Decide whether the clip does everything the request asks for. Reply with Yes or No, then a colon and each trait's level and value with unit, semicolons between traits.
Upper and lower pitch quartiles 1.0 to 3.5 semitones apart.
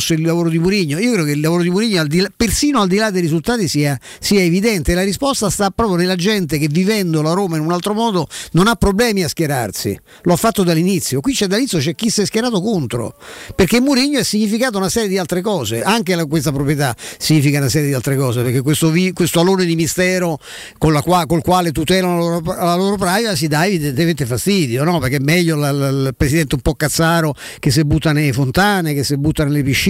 No: average, 4.3 semitones